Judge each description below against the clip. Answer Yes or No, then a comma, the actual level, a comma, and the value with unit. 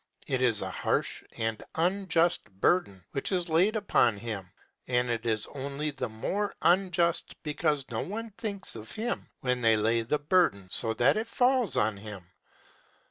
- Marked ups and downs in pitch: Yes, wide, 8.5 semitones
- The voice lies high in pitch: No, medium, 140 Hz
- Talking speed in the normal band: Yes, average, 160 wpm